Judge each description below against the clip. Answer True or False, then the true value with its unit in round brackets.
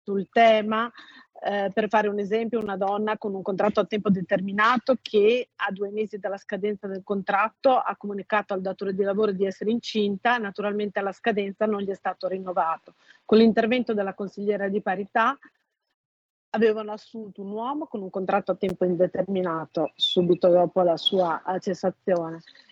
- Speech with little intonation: True (2.1 semitones)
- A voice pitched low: False (205 Hz)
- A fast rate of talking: False (160 wpm)